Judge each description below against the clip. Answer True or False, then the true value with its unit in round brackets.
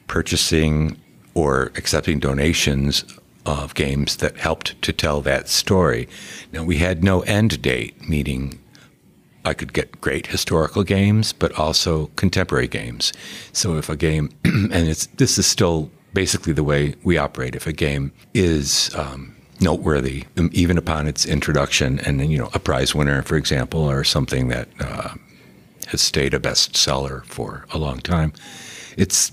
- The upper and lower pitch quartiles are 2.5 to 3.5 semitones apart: False (3.9 semitones)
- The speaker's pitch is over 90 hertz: False (80 Hz)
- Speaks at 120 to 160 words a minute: True (155 wpm)